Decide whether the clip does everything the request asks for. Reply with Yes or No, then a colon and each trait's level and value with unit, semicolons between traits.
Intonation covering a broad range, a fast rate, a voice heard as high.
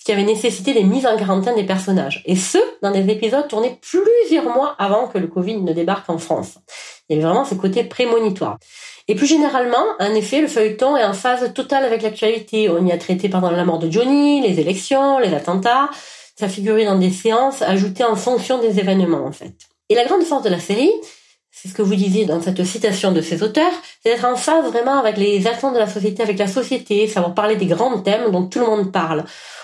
No: average, 4.5 semitones; fast, 230 wpm; high, 215 Hz